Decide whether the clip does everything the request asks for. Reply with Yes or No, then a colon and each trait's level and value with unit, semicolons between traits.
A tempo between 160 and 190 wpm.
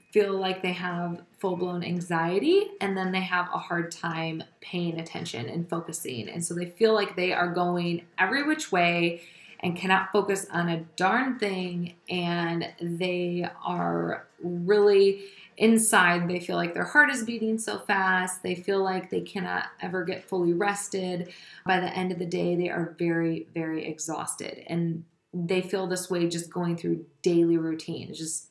Yes: average, 170 wpm